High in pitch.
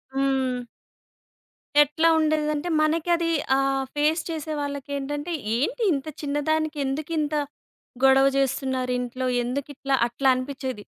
Yes: very high, 280 Hz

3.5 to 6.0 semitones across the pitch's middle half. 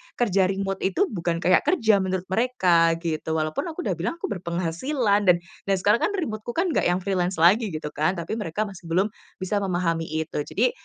Yes: average, 4.1 semitones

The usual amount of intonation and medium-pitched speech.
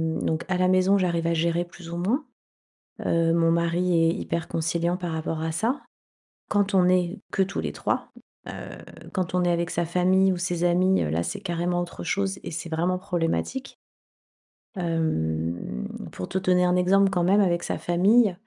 No: narrow, 1.9 semitones; medium, 175 Hz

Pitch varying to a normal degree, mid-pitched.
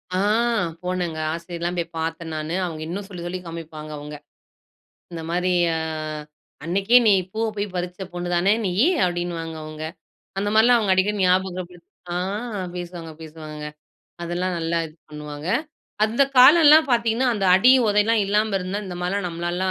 Yes: average, 3.4 semitones; medium, 180 Hz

